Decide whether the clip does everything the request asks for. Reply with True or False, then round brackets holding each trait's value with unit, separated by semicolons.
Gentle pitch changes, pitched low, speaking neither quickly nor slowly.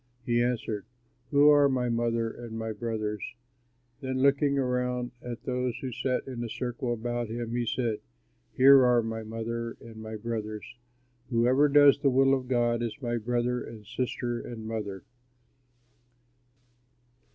True (2.1 semitones; 120 Hz; 150 wpm)